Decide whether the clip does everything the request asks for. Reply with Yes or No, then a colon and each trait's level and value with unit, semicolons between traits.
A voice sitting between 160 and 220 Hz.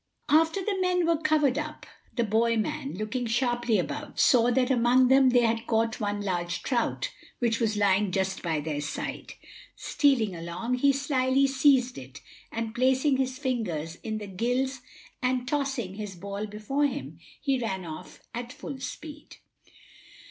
No: high, 240 Hz